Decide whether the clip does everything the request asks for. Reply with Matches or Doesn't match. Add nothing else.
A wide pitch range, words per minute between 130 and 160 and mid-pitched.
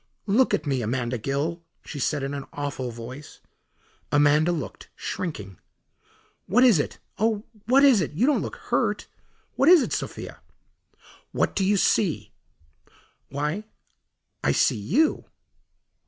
Matches